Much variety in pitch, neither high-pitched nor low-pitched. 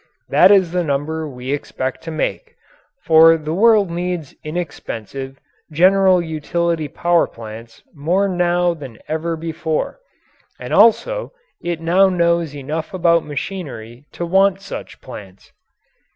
No: average, 3.5 semitones; medium, 165 Hz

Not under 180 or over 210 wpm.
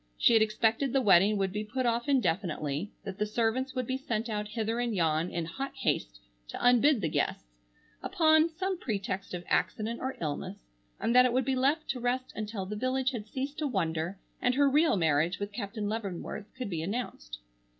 Yes: average, 200 wpm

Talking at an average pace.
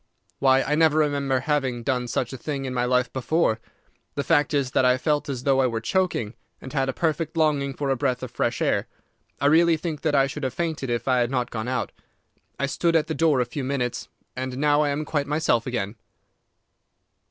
No: fast, 225 wpm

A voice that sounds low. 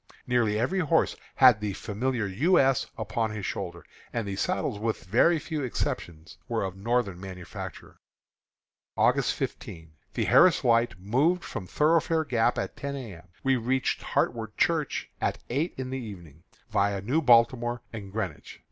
Yes: low, 115 Hz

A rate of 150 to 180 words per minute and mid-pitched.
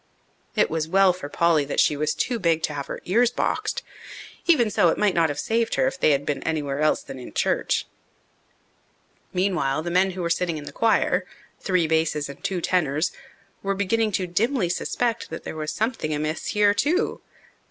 No: average, 195 wpm; medium, 175 Hz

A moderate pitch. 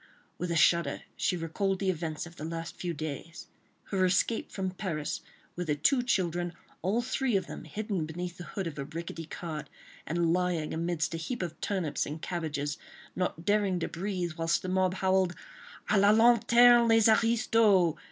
Yes: medium, 180 Hz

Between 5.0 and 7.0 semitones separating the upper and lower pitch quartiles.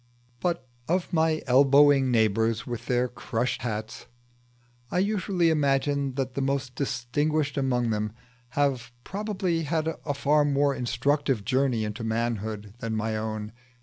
No: average, 4.3 semitones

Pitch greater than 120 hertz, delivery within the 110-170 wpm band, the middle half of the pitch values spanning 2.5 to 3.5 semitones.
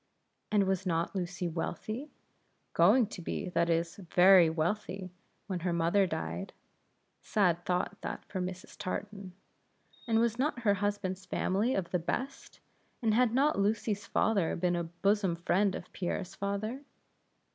Yes: high, 190 Hz; average, 145 wpm; average, 3.1 semitones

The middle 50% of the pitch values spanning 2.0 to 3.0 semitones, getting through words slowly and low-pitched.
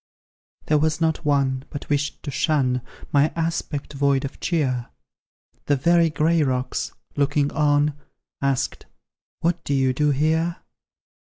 No: narrow, 2.4 semitones; slow, 125 wpm; medium, 145 Hz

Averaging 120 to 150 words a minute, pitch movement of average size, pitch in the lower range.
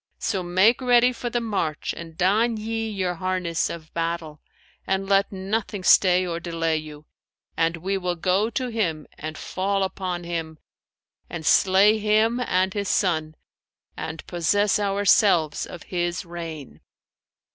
No: average, 145 wpm; average, 3.6 semitones; medium, 185 Hz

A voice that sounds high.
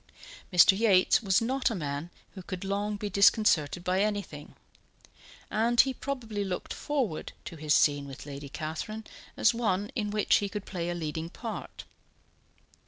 Yes: high, 195 Hz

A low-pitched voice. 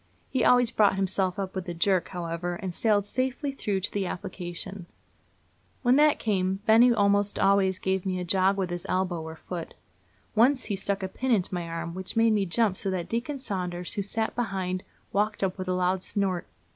No: high, 190 Hz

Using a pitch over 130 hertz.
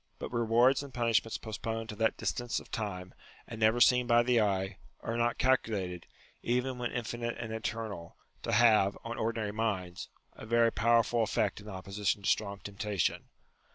No: low, 115 Hz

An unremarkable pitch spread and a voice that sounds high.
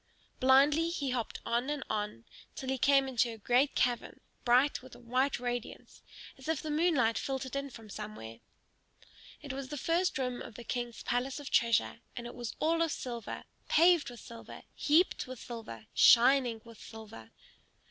Yes: average, 3.2 semitones; very high, 255 Hz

